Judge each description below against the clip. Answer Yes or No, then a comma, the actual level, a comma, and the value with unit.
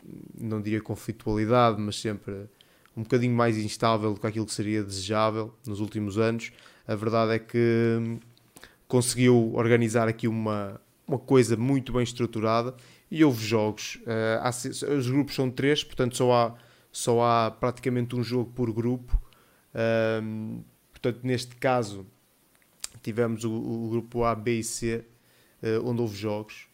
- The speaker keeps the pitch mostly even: Yes, narrow, 1.9 semitones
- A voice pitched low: Yes, low, 115 Hz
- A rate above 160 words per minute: No, average, 135 wpm